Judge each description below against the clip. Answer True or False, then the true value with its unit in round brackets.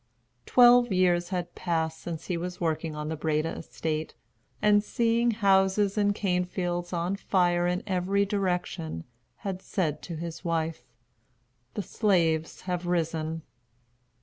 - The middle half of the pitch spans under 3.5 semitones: True (3.1 semitones)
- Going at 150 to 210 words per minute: False (135 wpm)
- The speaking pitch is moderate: True (180 Hz)